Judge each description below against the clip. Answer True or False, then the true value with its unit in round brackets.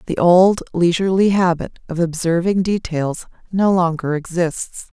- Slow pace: True (120 wpm)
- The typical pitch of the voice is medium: True (175 Hz)